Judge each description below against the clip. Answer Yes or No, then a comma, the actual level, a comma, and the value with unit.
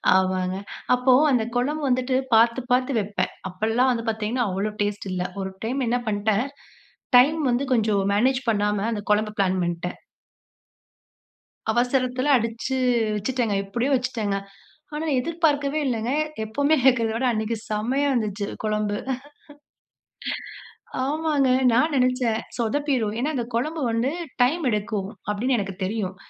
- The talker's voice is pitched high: Yes, high, 230 Hz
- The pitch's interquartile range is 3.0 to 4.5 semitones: Yes, average, 3.7 semitones